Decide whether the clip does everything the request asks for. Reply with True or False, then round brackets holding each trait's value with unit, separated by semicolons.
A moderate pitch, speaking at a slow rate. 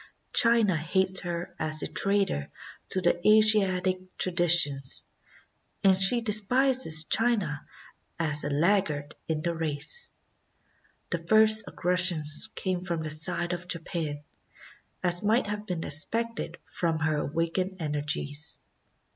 True (175 Hz; 120 wpm)